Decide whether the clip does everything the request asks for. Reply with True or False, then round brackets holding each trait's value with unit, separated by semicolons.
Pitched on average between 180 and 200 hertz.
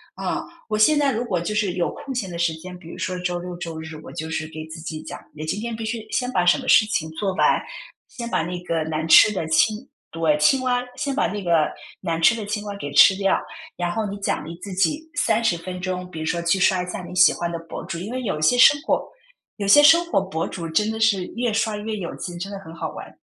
True (185 Hz)